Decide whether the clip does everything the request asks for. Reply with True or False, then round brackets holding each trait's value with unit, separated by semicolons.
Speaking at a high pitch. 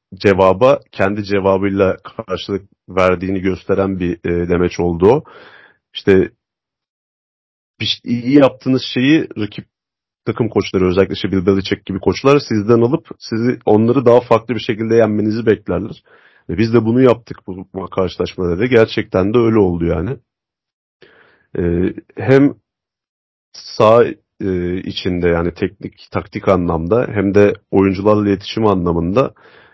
False (100 Hz)